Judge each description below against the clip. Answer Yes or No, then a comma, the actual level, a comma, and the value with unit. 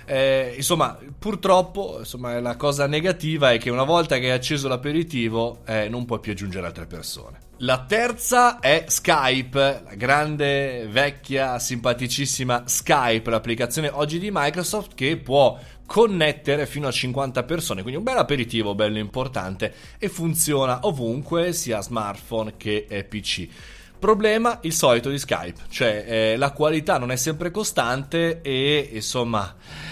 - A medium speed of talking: Yes, average, 140 wpm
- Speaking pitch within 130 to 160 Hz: Yes, low, 135 Hz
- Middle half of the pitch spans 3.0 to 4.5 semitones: No, average, 5.1 semitones